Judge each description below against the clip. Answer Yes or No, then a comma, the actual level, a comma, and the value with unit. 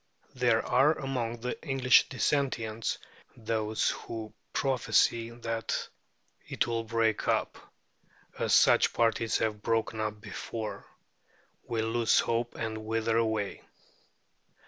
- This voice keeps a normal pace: No, slow, 110 wpm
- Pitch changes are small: Yes, narrow, 1.3 semitones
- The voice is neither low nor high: No, low, 115 Hz